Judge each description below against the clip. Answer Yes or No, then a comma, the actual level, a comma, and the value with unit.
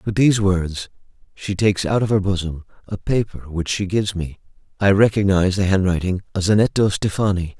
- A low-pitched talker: Yes, very low, 95 Hz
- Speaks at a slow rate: No, average, 175 wpm